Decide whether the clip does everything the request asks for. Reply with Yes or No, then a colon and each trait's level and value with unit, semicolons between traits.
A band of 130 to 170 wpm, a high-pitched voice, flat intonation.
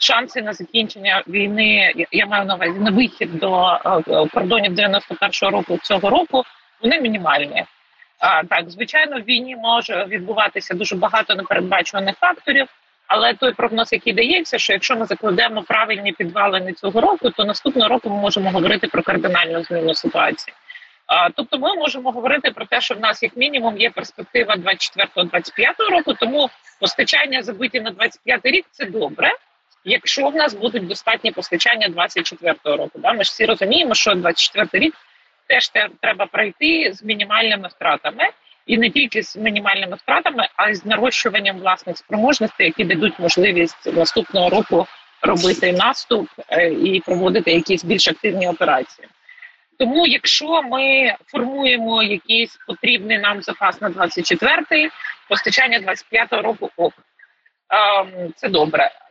No: average, 140 wpm; high, 220 Hz; average, 4.6 semitones